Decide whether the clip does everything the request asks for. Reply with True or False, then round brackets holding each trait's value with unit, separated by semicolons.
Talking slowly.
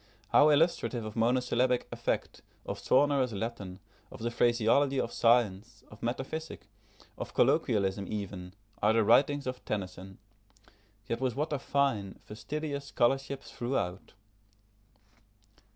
True (120 wpm)